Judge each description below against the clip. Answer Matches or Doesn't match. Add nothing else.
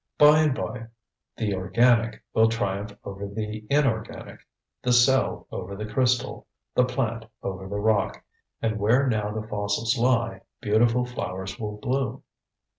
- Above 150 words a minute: Doesn't match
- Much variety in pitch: Doesn't match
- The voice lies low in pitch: Matches